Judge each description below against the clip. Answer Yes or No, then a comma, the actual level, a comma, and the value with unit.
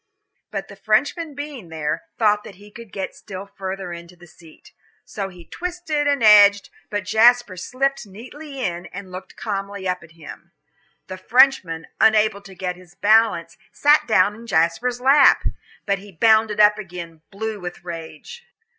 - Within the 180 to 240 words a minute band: No, average, 165 wpm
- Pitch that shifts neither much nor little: Yes, average, 4.5 semitones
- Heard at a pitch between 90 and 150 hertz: No, high, 205 Hz